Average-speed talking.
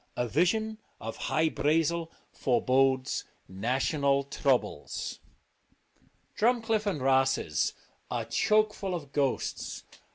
No: slow, 90 wpm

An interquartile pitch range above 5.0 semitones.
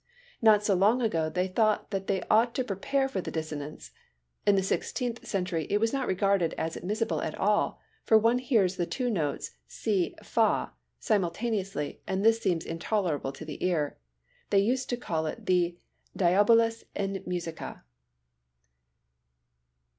No: average, 4.6 semitones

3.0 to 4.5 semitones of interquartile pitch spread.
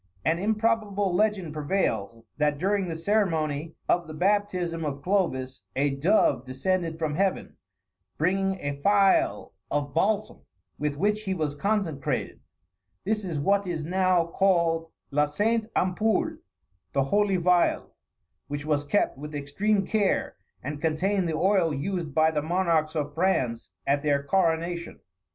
No: average, 4.9 semitones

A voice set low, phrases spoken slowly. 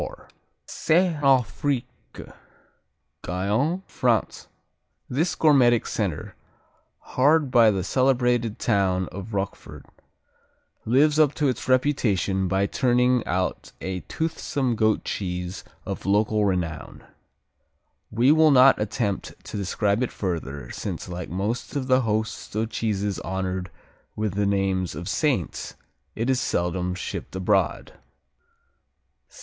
Yes: low, 110 Hz; slow, 115 wpm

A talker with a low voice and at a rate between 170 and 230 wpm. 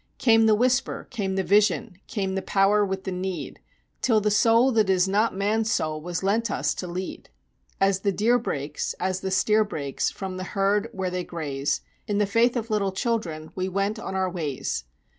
No: high, 195 Hz; average, 200 wpm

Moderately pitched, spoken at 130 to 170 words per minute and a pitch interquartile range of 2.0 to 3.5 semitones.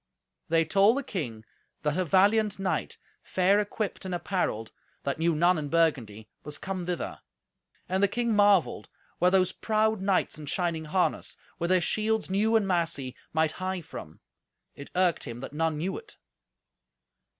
No: medium, 180 Hz; average, 160 wpm; average, 4.0 semitones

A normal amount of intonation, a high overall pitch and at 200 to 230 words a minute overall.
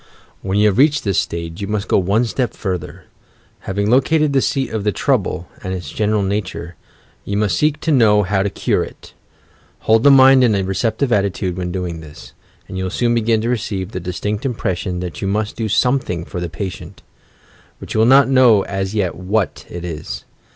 No: average, 4.0 semitones; low, 100 Hz; fast, 205 wpm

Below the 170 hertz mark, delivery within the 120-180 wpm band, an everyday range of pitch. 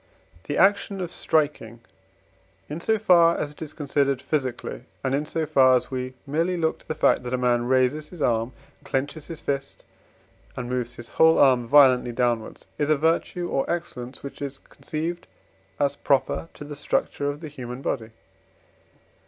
Yes: medium, 140 Hz; average, 175 wpm; average, 3.8 semitones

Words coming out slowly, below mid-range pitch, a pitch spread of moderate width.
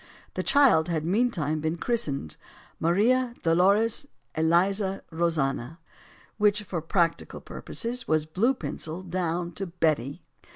No: slow, 115 wpm; medium, 175 Hz; average, 4.6 semitones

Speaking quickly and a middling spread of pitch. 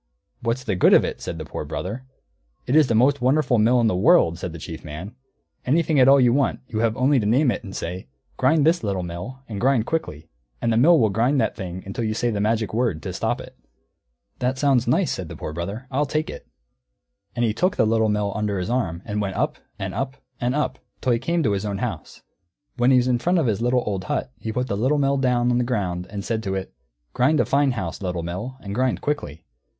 Yes: fast, 250 wpm; average, 4.9 semitones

